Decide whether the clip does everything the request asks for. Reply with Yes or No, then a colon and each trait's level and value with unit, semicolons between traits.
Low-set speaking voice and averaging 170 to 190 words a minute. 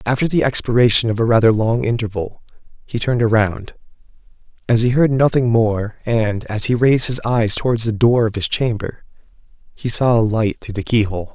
Yes: low, 115 Hz; average, 185 wpm